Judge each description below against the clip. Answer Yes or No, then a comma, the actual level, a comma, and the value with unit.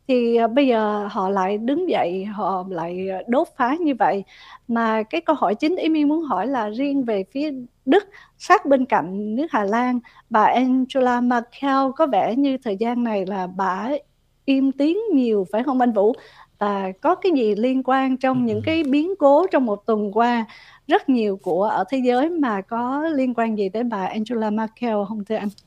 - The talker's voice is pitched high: Yes, high, 245 Hz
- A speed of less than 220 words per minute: Yes, average, 195 wpm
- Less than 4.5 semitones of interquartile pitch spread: No, average, 4.8 semitones